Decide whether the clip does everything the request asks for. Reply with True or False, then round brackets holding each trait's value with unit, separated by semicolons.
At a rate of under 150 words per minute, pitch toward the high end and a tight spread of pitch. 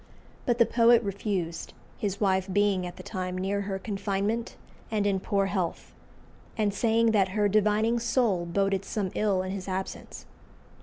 False (160 wpm; 200 Hz; 2.2 semitones)